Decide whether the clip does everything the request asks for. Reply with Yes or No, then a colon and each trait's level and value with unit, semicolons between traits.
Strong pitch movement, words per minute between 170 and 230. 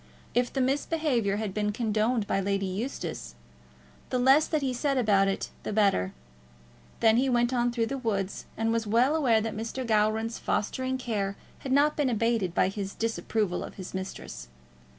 No: average, 3.9 semitones; average, 175 wpm